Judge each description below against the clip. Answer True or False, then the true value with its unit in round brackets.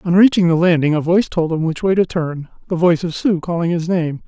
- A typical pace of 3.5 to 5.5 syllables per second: False (6.1 syllables/s)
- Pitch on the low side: False (170 Hz)